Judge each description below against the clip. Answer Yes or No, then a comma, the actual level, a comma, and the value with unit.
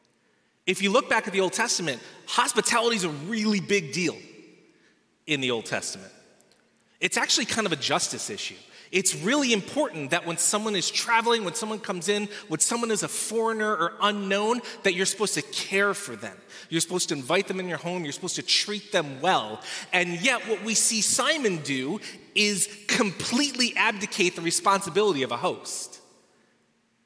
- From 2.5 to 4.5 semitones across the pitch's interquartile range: Yes, average, 3.7 semitones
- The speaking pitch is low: No, high, 200 Hz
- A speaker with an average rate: Yes, average, 175 wpm